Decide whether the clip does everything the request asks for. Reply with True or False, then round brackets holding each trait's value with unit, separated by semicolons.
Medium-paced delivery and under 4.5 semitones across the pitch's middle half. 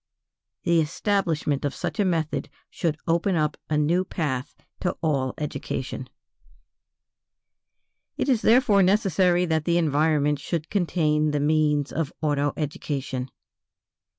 False (125 wpm; 3.0 semitones)